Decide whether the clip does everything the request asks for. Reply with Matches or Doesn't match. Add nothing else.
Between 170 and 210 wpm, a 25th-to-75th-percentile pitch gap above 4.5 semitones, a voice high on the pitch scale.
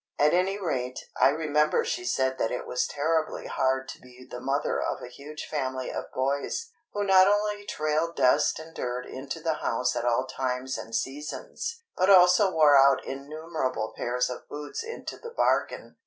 Doesn't match